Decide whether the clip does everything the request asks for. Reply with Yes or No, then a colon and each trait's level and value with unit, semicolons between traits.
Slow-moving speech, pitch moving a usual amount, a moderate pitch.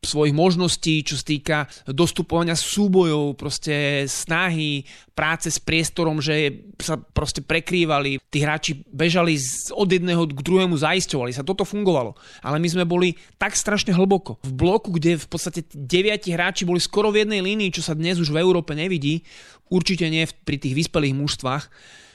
No: average, 155 wpm; average, 3.3 semitones; medium, 165 Hz